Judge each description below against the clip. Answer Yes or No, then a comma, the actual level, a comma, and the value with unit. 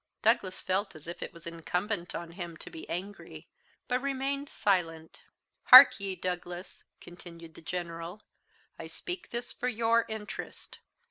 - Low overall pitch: No, medium, 185 Hz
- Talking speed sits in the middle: Yes, average, 145 wpm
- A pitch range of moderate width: Yes, average, 5.0 semitones